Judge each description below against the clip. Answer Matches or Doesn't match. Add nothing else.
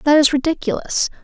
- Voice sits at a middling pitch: Doesn't match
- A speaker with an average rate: Matches